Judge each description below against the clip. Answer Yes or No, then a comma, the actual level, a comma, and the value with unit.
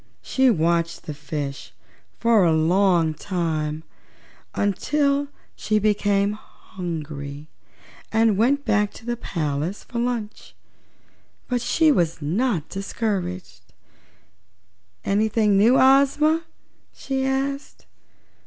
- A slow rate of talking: Yes, slow, 95 wpm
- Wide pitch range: Yes, wide, 6.8 semitones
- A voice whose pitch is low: No, high, 200 Hz